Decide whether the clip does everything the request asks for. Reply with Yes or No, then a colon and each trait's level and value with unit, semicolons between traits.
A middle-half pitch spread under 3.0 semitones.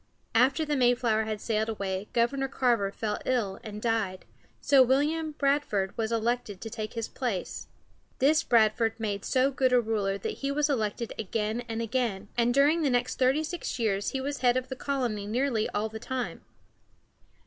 No: average, 3.5 semitones